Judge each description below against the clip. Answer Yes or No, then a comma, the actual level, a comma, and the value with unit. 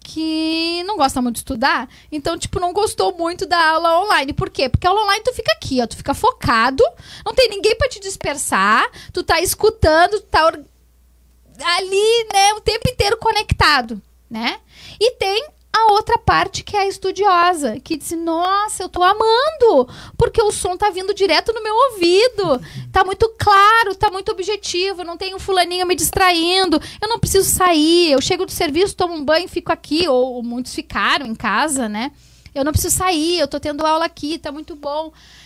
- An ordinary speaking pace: No, fast, 190 wpm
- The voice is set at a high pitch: Yes, very high, 365 Hz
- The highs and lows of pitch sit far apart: No, average, 4.6 semitones